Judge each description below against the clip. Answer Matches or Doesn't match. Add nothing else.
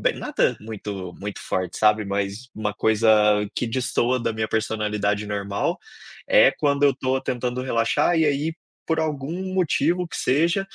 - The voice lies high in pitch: Doesn't match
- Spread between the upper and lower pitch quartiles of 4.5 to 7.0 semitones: Matches